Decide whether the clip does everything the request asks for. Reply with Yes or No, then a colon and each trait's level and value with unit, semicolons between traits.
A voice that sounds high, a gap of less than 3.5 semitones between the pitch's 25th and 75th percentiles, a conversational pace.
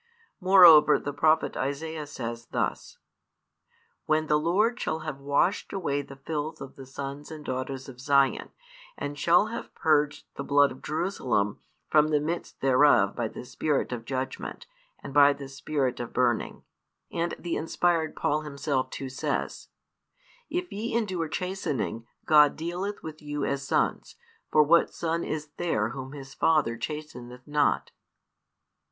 No: medium, 150 Hz; average, 3.0 semitones; average, 150 wpm